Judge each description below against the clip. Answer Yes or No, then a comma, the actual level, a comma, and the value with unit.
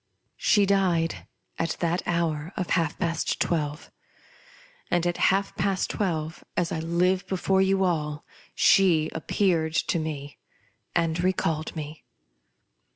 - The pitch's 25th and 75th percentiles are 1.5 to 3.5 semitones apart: Yes, average, 2.8 semitones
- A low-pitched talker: No, medium, 170 Hz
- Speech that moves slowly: Yes, slow, 125 wpm